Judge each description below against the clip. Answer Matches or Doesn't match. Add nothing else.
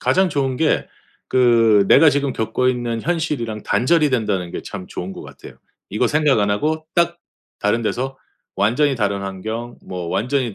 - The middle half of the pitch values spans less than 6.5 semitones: Matches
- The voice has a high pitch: Doesn't match